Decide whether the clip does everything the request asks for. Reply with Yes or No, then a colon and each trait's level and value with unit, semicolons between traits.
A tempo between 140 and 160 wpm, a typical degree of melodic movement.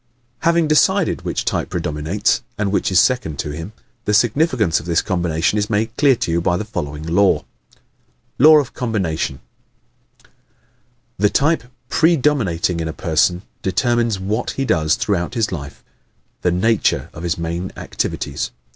No: average, 155 wpm; wide, 6.3 semitones